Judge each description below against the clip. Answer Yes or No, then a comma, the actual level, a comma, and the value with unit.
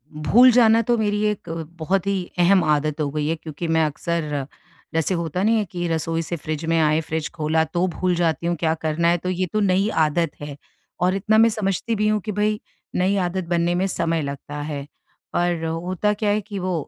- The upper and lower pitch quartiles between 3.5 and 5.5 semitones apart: Yes, average, 3.8 semitones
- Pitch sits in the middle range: Yes, medium, 175 Hz